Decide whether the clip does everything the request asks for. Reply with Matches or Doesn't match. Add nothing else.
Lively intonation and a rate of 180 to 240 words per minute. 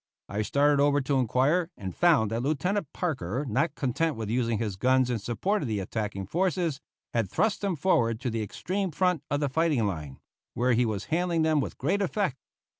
Matches